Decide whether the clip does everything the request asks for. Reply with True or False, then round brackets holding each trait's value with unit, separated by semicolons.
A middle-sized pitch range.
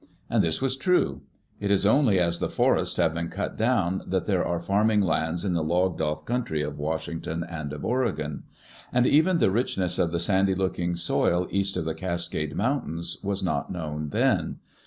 True (3.8 semitones)